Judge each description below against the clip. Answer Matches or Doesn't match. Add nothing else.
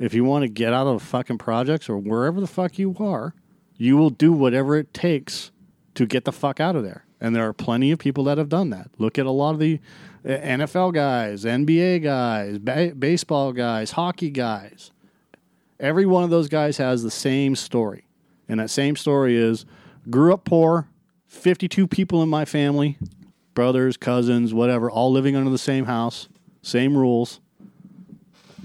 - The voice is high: Doesn't match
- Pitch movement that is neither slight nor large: Doesn't match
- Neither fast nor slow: Matches